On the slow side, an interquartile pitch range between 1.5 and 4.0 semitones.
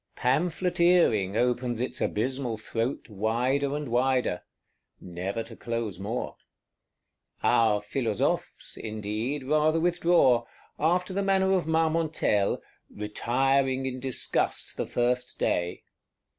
No: slow, 105 wpm; wide, 5.6 semitones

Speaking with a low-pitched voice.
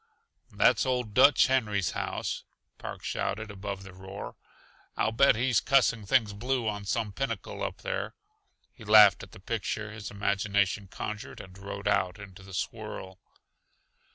Yes: low, 105 Hz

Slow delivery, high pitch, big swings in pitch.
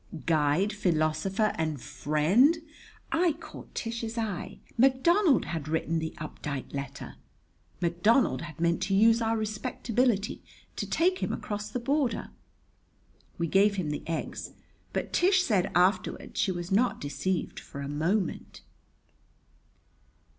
Yes: slow, 125 wpm; high, 195 Hz; wide, 6.4 semitones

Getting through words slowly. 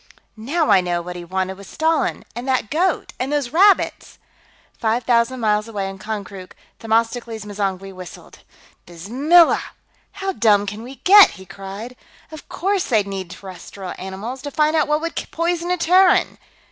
No: average, 160 wpm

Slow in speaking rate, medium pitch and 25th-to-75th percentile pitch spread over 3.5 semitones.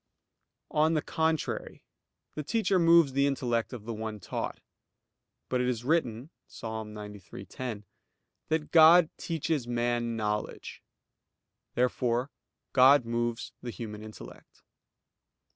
No: slow, 110 wpm; low, 125 Hz; average, 5.3 semitones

